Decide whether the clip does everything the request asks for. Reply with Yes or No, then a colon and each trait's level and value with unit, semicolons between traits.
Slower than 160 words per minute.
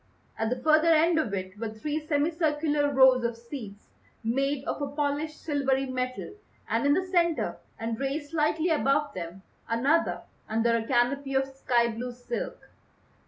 No: average, 165 wpm